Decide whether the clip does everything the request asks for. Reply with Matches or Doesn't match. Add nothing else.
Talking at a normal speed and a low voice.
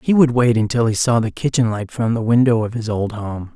Doesn't match